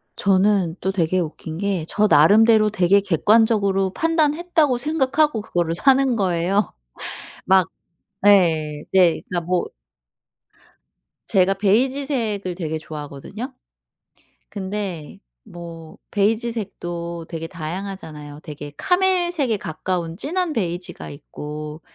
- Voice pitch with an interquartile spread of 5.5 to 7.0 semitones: No, average, 5.1 semitones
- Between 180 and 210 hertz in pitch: Yes, high, 190 Hz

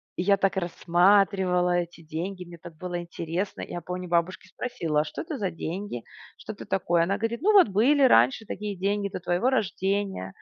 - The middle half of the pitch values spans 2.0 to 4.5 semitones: Yes, average, 2.8 semitones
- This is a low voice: No, medium, 185 Hz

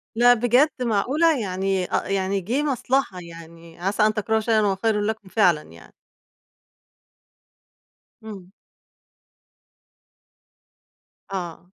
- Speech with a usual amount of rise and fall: Yes, average, 3.9 semitones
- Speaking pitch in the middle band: No, high, 205 Hz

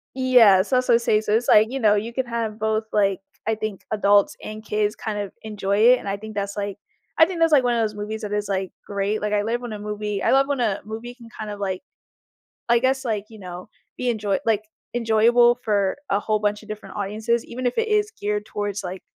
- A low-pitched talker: No, high, 215 Hz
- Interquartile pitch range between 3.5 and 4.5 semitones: No, narrow, 2.4 semitones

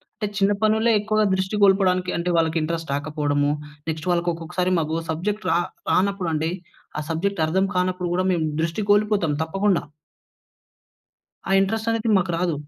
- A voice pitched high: No, medium, 180 Hz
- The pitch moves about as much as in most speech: Yes, average, 3.5 semitones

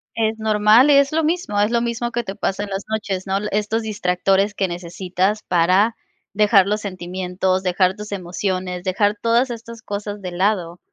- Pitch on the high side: Yes, high, 205 Hz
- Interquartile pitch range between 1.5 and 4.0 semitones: Yes, average, 2.9 semitones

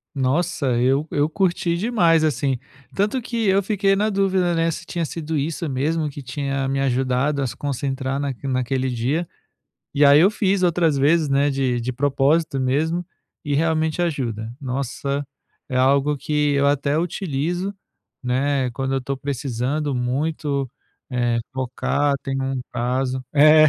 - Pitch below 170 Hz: Yes, medium, 140 Hz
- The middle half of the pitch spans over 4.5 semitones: No, average, 3.6 semitones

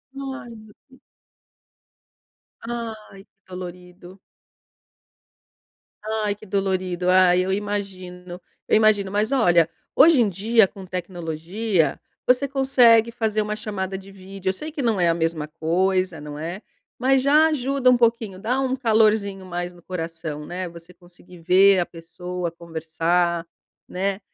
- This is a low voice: No, high, 190 Hz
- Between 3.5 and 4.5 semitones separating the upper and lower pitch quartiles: Yes, average, 3.9 semitones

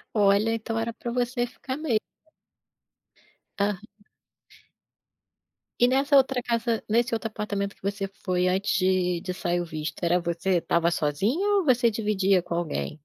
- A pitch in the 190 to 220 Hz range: Yes, high, 205 Hz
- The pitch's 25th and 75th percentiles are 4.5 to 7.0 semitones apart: Yes, average, 4.8 semitones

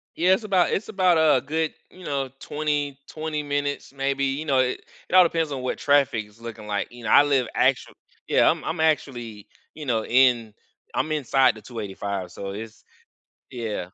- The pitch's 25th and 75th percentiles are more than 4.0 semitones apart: Yes, average, 5.2 semitones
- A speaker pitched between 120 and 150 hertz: Yes, low, 135 Hz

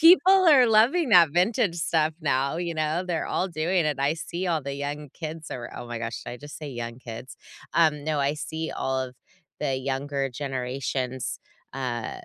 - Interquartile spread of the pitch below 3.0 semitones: No, average, 4.2 semitones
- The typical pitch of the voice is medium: Yes, medium, 150 Hz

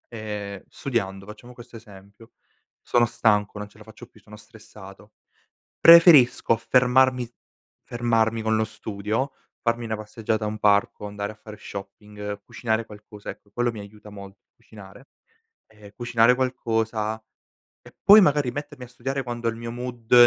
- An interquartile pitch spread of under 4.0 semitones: Yes, narrow, 2.6 semitones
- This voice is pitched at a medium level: No, low, 110 Hz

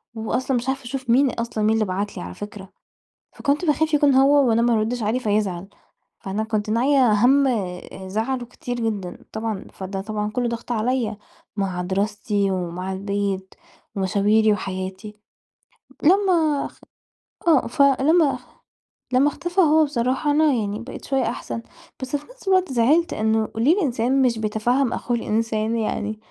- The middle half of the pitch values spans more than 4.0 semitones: Yes, average, 4.4 semitones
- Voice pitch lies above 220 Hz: Yes, high, 230 Hz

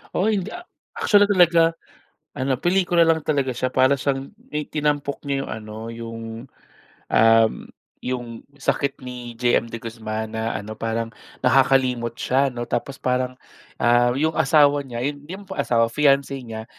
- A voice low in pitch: Yes, low, 130 Hz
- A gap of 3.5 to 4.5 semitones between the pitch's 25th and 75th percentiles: Yes, average, 4.0 semitones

